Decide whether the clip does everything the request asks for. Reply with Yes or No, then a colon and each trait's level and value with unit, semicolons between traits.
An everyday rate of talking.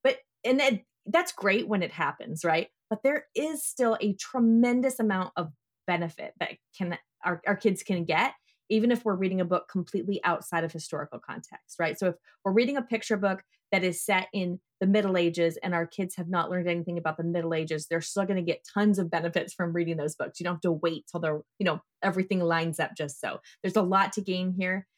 No: fast, 225 wpm